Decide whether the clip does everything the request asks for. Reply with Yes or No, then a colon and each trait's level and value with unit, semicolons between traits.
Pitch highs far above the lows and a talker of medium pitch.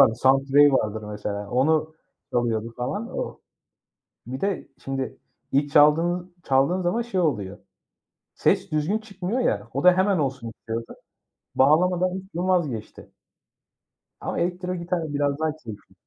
Yes: wide, 6.0 semitones; medium, 150 Hz